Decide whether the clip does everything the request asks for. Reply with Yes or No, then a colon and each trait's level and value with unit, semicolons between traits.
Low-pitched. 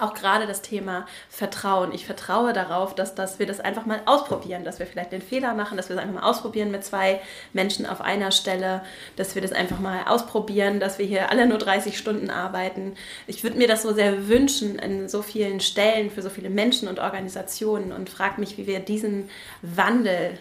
No: high, 195 Hz